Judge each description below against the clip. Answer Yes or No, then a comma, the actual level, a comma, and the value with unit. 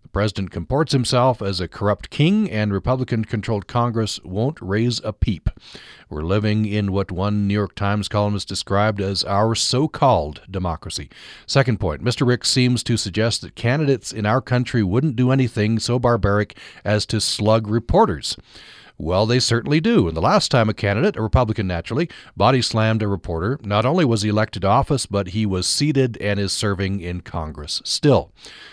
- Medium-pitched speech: No, low, 110 Hz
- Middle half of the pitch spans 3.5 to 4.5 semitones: Yes, average, 3.8 semitones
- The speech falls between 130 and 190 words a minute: Yes, average, 180 wpm